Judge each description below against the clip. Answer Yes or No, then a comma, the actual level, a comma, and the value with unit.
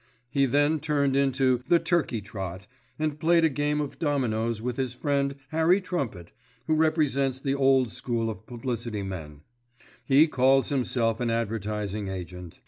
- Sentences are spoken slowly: No, average, 150 wpm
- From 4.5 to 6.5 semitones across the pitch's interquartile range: Yes, average, 4.8 semitones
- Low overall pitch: Yes, low, 130 Hz